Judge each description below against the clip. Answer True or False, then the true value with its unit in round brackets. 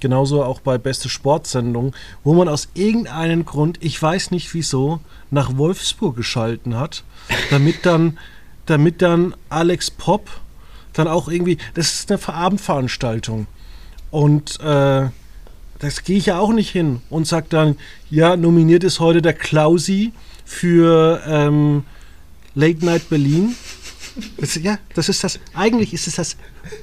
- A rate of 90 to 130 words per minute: False (145 wpm)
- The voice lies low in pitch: False (160 Hz)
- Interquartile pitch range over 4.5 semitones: False (3.7 semitones)